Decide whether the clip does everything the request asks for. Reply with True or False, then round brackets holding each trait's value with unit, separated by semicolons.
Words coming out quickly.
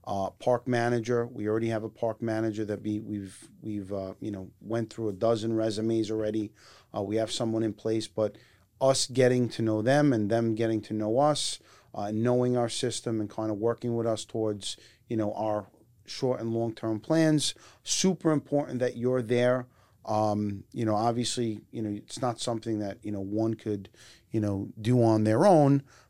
False (195 wpm)